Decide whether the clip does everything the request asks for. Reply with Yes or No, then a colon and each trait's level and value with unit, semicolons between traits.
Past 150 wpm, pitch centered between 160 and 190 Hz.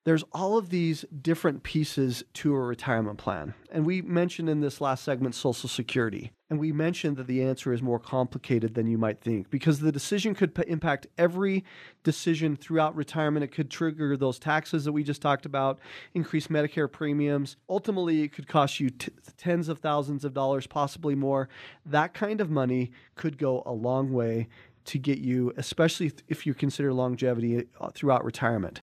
No: average, 180 wpm; medium, 145 Hz